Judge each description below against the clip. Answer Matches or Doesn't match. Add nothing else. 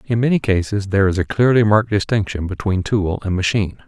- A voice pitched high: Doesn't match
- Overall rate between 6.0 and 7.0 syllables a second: Matches